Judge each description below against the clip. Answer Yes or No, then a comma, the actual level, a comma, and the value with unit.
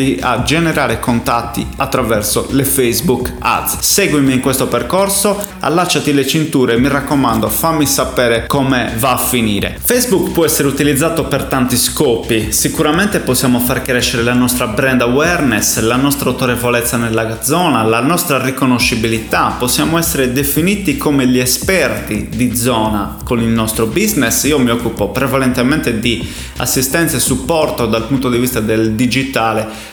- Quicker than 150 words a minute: No, average, 140 wpm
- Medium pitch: No, low, 130 Hz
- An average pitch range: Yes, average, 3.7 semitones